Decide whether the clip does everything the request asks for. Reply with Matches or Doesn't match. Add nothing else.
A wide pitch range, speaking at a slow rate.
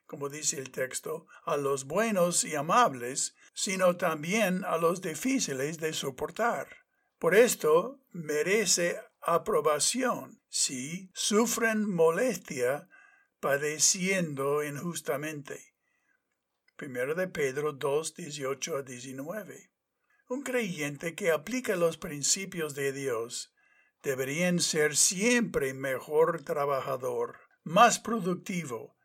Matches